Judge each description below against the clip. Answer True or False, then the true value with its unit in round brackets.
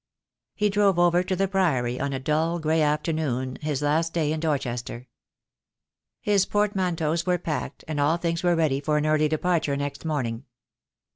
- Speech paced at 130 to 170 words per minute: True (165 wpm)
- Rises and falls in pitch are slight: False (3.3 semitones)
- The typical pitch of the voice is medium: True (155 Hz)